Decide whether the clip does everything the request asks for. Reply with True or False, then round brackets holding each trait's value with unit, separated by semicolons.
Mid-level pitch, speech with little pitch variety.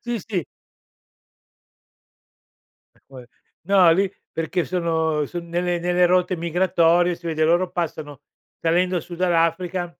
True (175 Hz; 1.6 semitones)